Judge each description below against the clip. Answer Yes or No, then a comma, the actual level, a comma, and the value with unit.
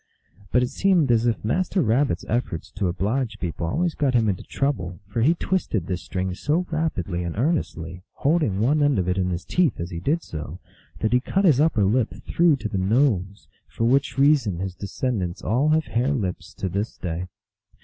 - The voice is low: Yes, low, 115 Hz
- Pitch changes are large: Yes, wide, 7.6 semitones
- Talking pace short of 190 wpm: No, average, 200 wpm